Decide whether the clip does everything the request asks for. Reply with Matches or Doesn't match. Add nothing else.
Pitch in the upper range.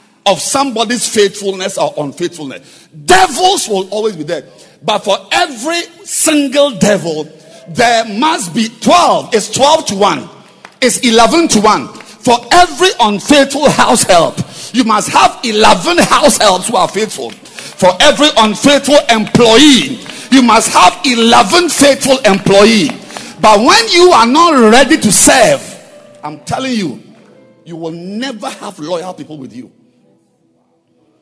Matches